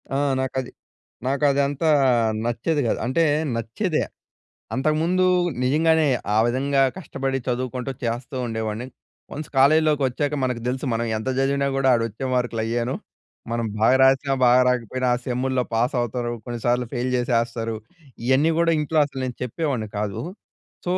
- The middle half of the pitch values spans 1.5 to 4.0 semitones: Yes, average, 2.9 semitones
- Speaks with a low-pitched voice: Yes, low, 130 Hz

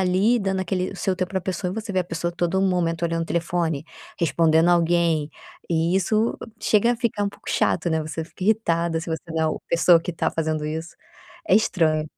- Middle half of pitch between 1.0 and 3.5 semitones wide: Yes, average, 2.7 semitones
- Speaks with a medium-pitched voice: Yes, medium, 170 Hz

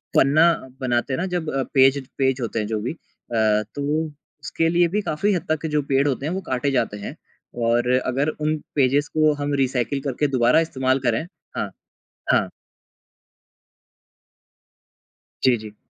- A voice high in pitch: No, low, 135 Hz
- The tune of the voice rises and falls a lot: No, average, 3.8 semitones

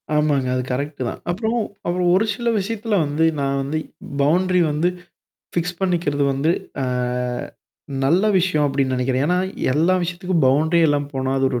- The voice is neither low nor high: Yes, medium, 155 Hz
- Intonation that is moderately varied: Yes, average, 4.6 semitones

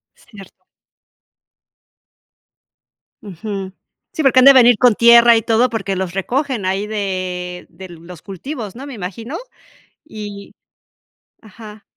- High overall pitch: Yes, high, 210 Hz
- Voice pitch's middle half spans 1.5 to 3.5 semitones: No, average, 3.9 semitones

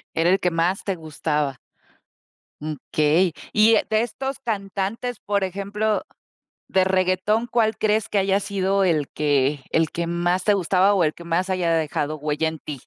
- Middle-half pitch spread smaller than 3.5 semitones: No, average, 4.0 semitones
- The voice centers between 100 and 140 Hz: No, medium, 185 Hz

